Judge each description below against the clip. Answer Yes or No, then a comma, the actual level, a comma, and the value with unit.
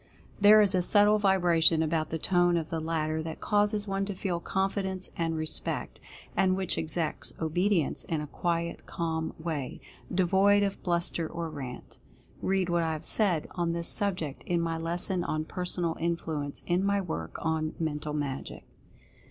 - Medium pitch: Yes, medium, 170 Hz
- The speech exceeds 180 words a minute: No, average, 165 wpm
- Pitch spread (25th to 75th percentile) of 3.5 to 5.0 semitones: No, average, 3.1 semitones